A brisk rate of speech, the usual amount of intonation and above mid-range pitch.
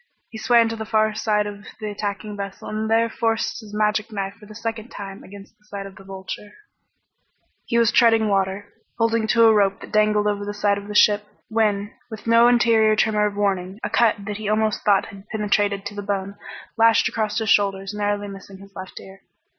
No: fast, 210 wpm; narrow, 1.5 semitones; high, 210 Hz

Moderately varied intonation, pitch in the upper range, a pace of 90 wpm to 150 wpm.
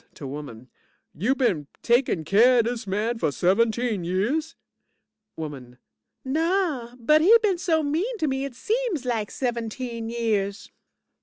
No: wide, 7.0 semitones; high, 235 Hz; average, 140 wpm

